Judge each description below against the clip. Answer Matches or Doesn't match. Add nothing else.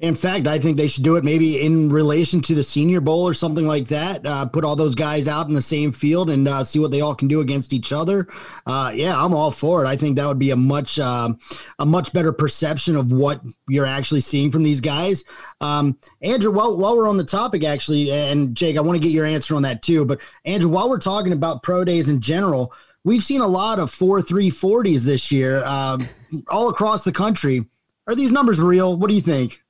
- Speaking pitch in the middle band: Matches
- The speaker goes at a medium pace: Doesn't match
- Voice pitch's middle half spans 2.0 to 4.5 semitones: Matches